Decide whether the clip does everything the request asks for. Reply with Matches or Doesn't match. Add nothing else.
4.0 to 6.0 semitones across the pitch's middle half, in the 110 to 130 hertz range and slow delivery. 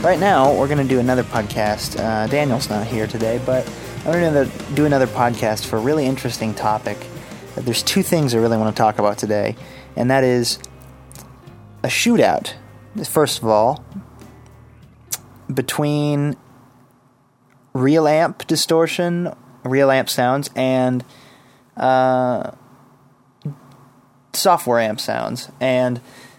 Doesn't match